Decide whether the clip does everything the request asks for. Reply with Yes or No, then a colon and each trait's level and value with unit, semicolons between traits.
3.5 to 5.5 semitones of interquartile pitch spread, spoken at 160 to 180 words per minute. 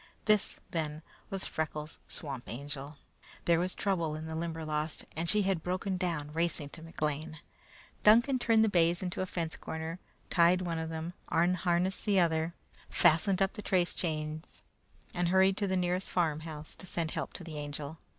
No: average, 2.8 semitones; average, 170 wpm